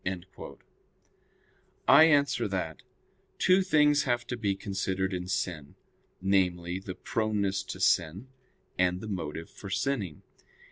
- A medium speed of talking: No, slow, 120 wpm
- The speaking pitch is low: Yes, very low, 95 Hz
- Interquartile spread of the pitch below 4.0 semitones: No, average, 4.8 semitones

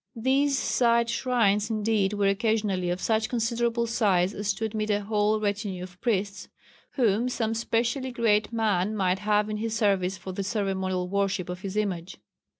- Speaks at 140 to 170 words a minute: Yes, average, 165 wpm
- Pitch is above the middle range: Yes, high, 210 Hz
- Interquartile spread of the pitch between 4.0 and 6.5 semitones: No, average, 2.7 semitones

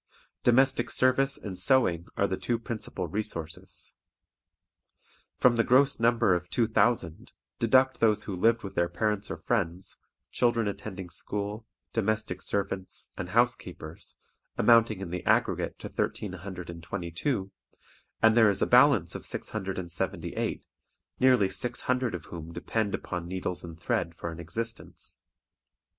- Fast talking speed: No, slow, 135 wpm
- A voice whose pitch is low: Yes, low, 105 Hz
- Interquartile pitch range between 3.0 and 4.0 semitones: No, average, 4.8 semitones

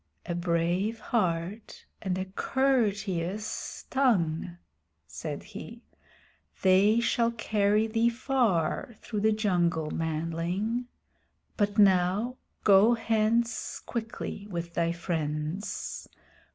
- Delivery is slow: Yes, slow, 95 wpm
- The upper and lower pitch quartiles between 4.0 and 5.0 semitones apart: Yes, average, 4.7 semitones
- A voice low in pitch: No, high, 200 Hz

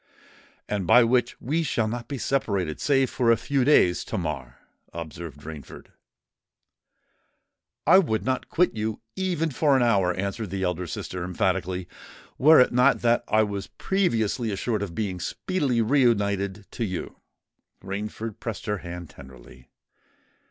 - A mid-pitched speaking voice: No, low, 110 Hz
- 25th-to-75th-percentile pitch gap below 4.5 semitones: No, wide, 5.6 semitones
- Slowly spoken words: No, average, 145 wpm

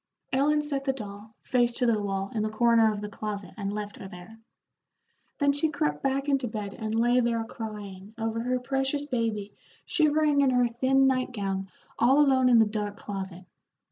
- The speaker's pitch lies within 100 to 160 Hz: No, high, 230 Hz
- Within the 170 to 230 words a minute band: Yes, average, 190 wpm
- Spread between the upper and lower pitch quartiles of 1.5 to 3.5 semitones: No, average, 4.4 semitones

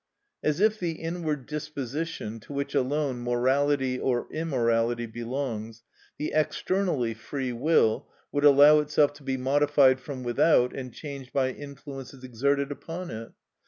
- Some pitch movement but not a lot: Yes, average, 3.3 semitones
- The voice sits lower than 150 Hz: Yes, medium, 140 Hz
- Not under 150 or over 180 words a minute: No, slow, 135 wpm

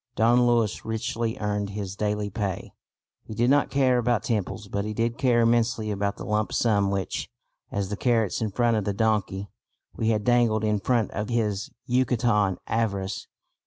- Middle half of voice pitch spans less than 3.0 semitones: Yes, narrow, 2.4 semitones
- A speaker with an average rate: Yes, average, 175 wpm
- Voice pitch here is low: Yes, low, 110 Hz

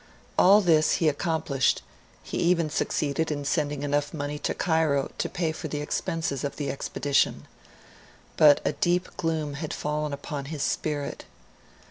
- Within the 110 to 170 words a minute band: Yes, average, 150 wpm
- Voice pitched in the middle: Yes, medium, 150 Hz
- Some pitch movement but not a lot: No, narrow, 2.1 semitones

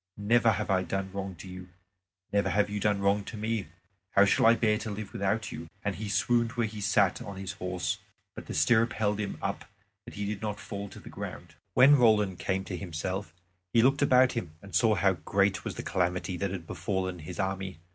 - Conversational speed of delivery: No, fast, 220 wpm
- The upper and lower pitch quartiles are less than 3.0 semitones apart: Yes, narrow, 2.4 semitones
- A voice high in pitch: No, low, 100 Hz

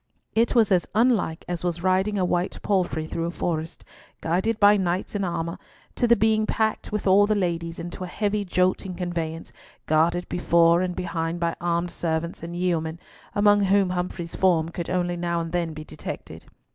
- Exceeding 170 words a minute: Yes, average, 185 wpm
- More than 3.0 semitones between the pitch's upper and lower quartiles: No, average, 2.7 semitones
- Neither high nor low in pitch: Yes, medium, 175 Hz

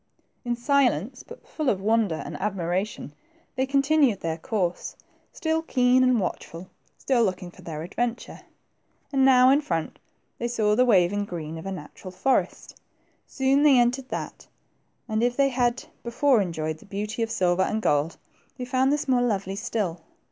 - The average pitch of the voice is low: No, high, 225 Hz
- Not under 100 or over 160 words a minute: No, average, 170 wpm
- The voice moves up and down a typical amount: No, wide, 5.8 semitones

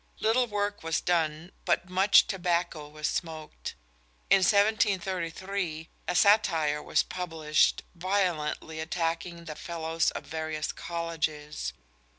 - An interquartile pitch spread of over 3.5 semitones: No, average, 3.1 semitones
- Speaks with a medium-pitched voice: Yes, medium, 170 Hz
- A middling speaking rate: No, slow, 110 wpm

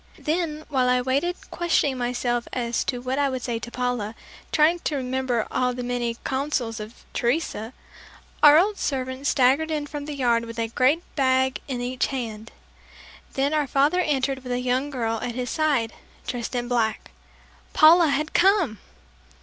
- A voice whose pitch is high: Yes, very high, 260 Hz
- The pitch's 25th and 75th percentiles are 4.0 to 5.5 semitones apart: No, average, 3.3 semitones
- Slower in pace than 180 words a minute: Yes, average, 170 wpm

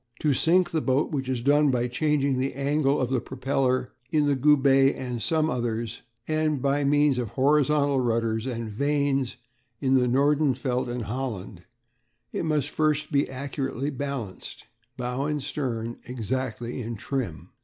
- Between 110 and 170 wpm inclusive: Yes, average, 155 wpm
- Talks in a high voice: No, low, 135 Hz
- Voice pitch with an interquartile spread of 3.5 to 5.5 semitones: No, average, 2.8 semitones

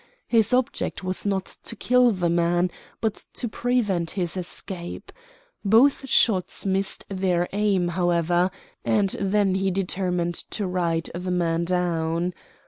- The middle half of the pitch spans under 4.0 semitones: Yes, narrow, 2.6 semitones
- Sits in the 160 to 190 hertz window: Yes, medium, 185 Hz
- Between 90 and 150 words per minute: Yes, slow, 135 wpm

